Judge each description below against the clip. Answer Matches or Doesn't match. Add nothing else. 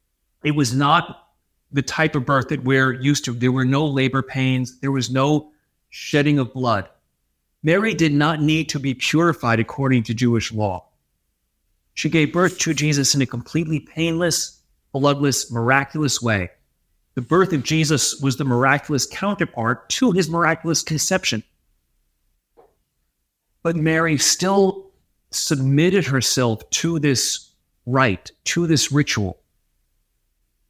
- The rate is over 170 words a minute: Doesn't match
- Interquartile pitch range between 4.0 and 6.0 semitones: Matches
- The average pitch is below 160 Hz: Matches